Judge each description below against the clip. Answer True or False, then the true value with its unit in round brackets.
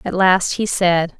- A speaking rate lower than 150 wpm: False (200 wpm)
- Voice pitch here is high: False (180 Hz)